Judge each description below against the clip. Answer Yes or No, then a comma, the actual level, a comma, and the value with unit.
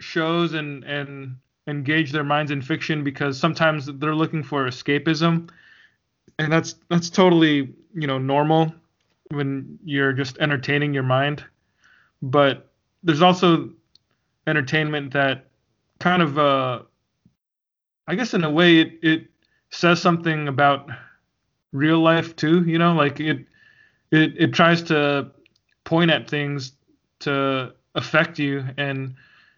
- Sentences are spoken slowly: Yes, slow, 130 wpm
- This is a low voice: No, medium, 150 Hz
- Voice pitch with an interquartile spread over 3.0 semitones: No, average, 2.7 semitones